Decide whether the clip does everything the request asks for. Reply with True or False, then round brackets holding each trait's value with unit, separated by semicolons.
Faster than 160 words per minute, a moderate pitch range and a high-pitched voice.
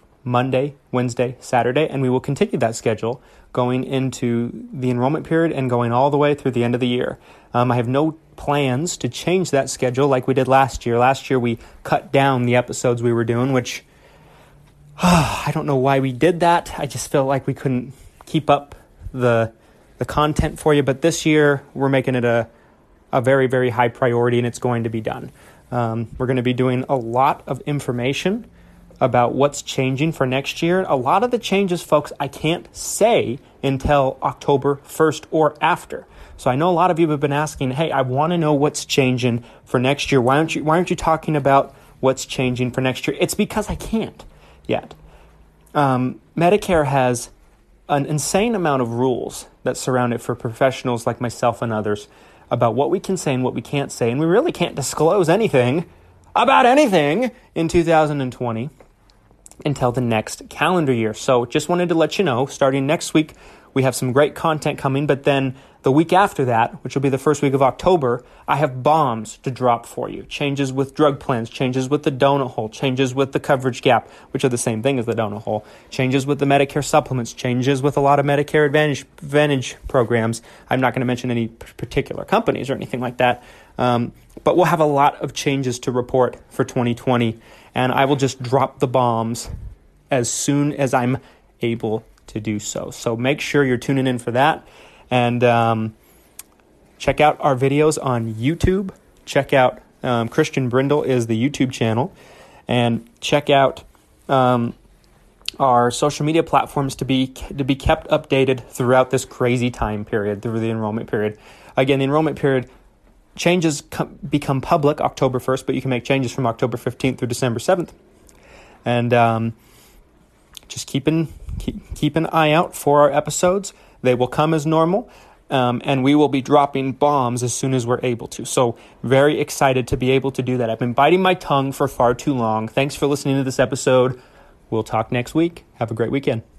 False (195 wpm; 3.1 semitones; 135 Hz)